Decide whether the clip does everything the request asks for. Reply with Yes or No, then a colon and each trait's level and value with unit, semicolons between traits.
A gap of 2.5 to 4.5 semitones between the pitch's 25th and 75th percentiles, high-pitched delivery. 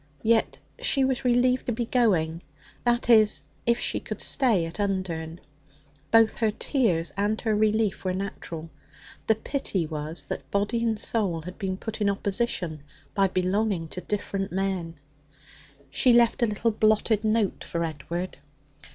Yes: average, 4.0 semitones; high, 205 Hz